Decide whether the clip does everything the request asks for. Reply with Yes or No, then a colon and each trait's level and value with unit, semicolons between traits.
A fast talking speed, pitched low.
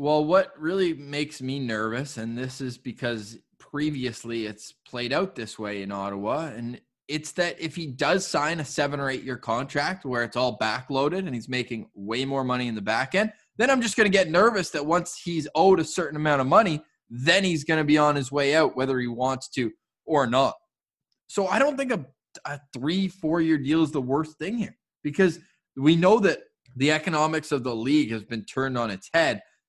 No: fast, 210 wpm; medium, 145 Hz